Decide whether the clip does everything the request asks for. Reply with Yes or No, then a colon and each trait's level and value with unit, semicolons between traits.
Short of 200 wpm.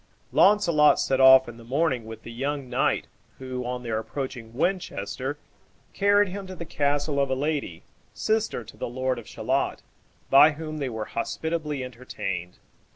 Yes: average, 160 wpm